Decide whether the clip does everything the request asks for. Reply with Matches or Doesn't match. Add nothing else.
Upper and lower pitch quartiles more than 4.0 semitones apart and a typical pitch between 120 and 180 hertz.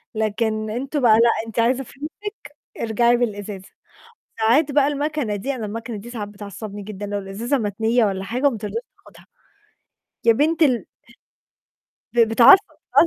Doesn't match